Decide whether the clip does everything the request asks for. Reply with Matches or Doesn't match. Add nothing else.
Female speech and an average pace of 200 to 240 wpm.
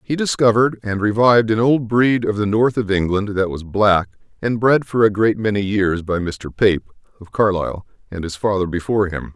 Doesn't match